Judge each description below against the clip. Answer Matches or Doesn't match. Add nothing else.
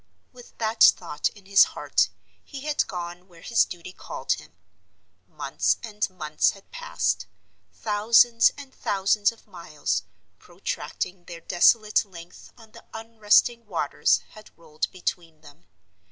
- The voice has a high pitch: Matches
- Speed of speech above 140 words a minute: Doesn't match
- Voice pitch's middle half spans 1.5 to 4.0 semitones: Doesn't match